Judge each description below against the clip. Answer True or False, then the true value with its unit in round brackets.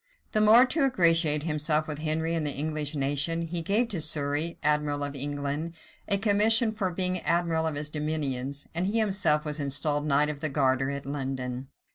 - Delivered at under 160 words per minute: False (185 wpm)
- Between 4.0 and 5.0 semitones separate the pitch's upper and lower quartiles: False (3.1 semitones)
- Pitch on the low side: False (155 Hz)